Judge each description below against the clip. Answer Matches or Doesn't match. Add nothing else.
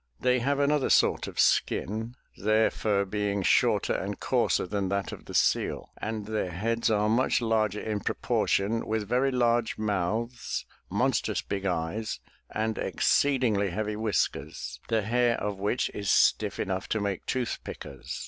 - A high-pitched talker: Doesn't match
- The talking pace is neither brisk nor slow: Matches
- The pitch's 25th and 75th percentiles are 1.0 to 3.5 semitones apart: Matches